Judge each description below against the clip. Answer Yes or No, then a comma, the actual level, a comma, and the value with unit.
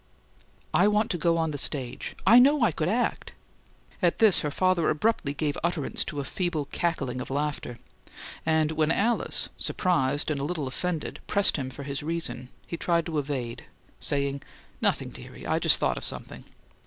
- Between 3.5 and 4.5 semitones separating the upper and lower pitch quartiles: Yes, average, 4.0 semitones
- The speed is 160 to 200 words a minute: Yes, average, 180 wpm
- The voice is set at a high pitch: No, medium, 155 Hz